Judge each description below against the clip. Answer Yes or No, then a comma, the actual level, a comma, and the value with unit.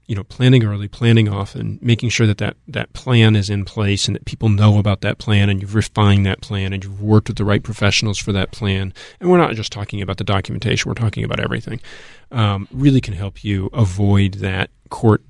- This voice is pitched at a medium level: No, low, 105 Hz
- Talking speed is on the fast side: Yes, fast, 225 wpm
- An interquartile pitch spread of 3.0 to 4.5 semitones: No, narrow, 2.4 semitones